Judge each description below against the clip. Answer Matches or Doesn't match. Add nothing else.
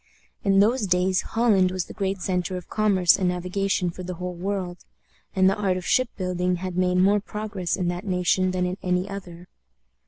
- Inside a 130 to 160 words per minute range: Doesn't match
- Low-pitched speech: Doesn't match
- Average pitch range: Doesn't match